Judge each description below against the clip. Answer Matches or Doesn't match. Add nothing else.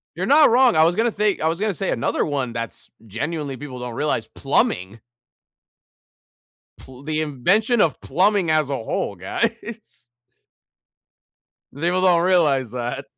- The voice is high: Doesn't match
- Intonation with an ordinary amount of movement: Doesn't match